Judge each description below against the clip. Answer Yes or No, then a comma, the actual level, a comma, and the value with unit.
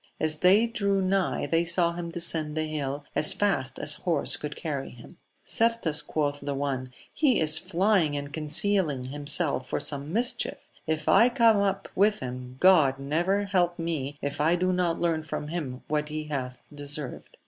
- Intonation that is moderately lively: Yes, average, 4.3 semitones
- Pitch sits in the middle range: Yes, medium, 155 Hz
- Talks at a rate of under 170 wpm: No, average, 175 wpm